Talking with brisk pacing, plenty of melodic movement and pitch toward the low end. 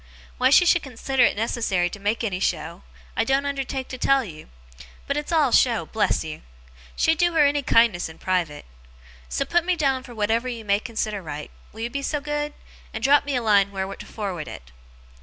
No: fast, 210 wpm; wide, 5.8 semitones; high, 235 Hz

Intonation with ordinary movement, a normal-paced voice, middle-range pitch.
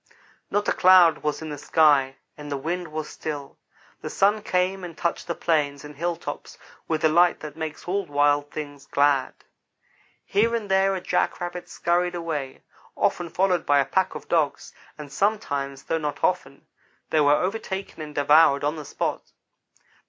Yes: average, 3.6 semitones; average, 170 wpm; medium, 160 Hz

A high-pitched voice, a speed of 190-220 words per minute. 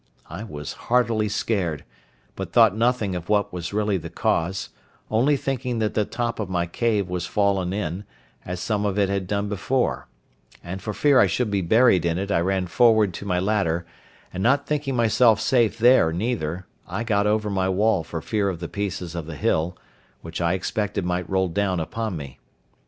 No: low, 100 Hz; average, 195 wpm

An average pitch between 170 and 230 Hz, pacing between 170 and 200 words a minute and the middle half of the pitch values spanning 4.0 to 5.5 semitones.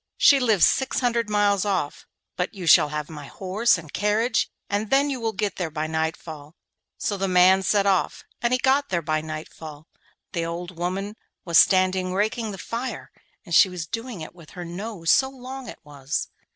Yes: high, 190 Hz; average, 190 wpm; average, 5.1 semitones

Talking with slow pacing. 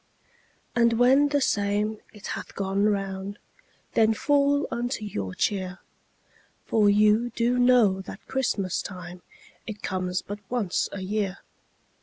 Yes: slow, 130 wpm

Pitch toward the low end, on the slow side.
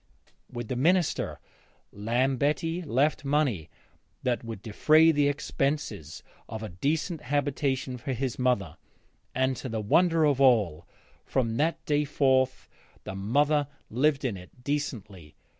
Yes: low, 130 Hz; slow, 130 wpm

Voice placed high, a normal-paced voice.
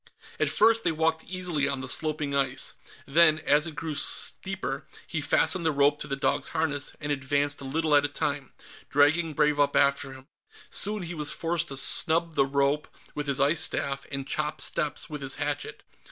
No: medium, 145 Hz; average, 195 wpm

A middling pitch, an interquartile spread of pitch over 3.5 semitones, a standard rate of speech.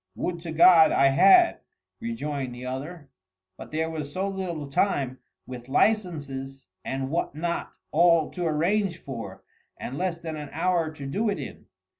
Yes: medium, 160 Hz; average, 4.6 semitones; average, 160 wpm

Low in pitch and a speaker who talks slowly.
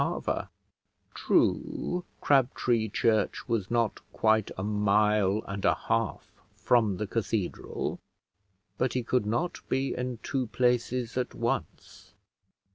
Yes: low, 115 Hz; slow, 115 wpm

